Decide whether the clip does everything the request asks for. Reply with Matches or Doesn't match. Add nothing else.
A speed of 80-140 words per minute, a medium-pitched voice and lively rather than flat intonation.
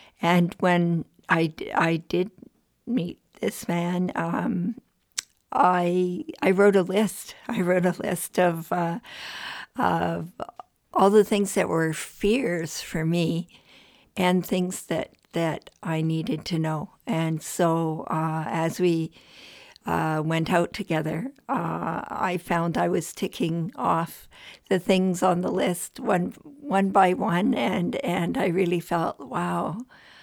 Doesn't match